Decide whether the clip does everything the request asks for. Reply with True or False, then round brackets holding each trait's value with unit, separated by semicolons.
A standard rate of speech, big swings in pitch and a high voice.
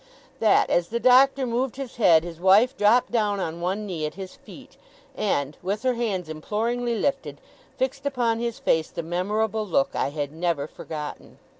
True (175 wpm; 5.9 semitones; 210 Hz)